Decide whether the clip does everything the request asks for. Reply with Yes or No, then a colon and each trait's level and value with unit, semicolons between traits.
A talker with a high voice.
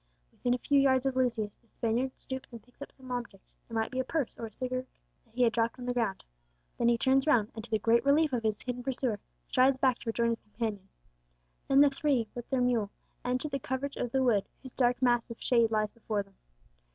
Yes: high, 245 Hz